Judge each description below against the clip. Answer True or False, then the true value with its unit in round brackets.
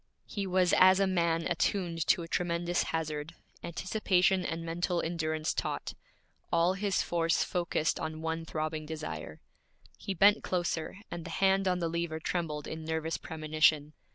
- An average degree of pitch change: False (2.2 semitones)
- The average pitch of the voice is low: False (165 Hz)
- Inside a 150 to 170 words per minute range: True (155 wpm)